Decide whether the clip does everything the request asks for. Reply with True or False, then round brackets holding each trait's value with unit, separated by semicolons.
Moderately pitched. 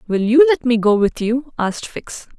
False (245 Hz)